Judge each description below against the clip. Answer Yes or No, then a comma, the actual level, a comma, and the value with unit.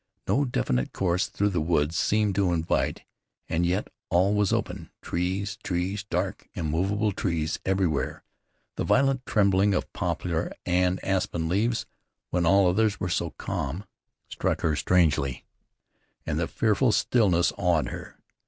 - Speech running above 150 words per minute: No, average, 140 wpm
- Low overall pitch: Yes, very low, 90 Hz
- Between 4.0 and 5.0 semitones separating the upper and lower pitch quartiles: No, average, 3.2 semitones